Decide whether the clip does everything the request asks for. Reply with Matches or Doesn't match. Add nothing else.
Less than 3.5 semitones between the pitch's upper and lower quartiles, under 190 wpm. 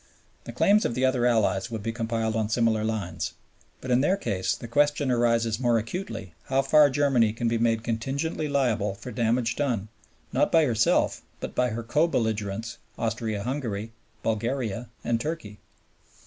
Matches